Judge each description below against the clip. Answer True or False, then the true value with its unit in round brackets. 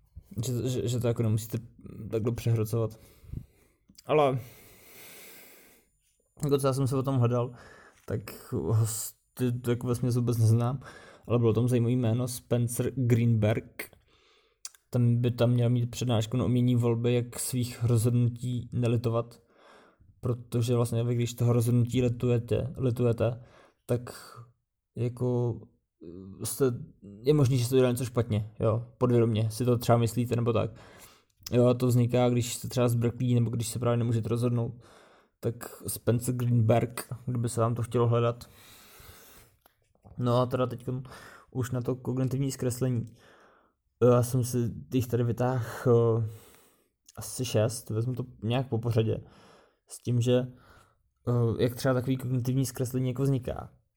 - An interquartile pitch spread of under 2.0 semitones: True (1.6 semitones)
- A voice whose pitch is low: True (120 Hz)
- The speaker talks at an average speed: True (140 wpm)